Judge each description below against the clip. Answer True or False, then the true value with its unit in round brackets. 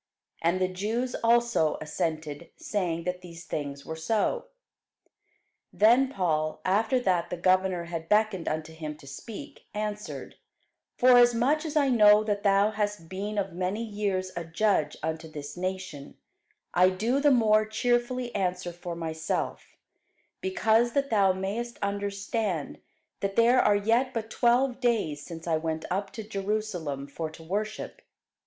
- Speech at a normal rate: True (145 wpm)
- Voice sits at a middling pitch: False (200 Hz)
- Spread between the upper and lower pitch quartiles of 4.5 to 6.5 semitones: True (5.2 semitones)